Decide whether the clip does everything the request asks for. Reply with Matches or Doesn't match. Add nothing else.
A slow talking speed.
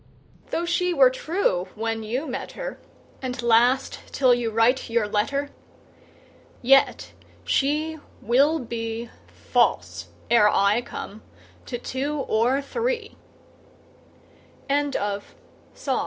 Matches